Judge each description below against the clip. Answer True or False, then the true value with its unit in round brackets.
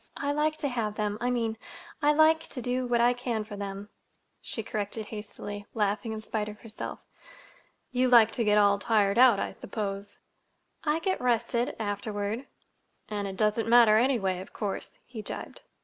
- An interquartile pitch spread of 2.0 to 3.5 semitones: True (3.1 semitones)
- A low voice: False (220 Hz)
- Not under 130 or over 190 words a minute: True (165 wpm)